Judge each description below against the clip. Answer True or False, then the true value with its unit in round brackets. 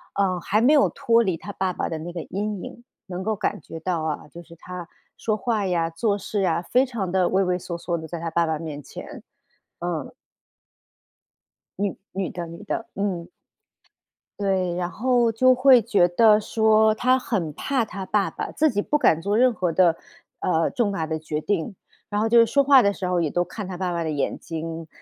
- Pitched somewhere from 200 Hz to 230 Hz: False (190 Hz)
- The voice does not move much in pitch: False (4.4 semitones)